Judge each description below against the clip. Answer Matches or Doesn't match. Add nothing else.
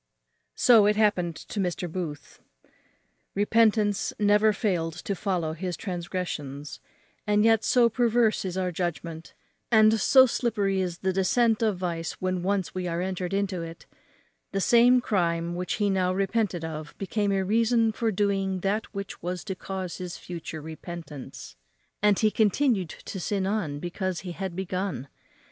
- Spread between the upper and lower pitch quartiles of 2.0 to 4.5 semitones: Matches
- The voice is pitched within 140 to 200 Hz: Matches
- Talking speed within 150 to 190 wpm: Matches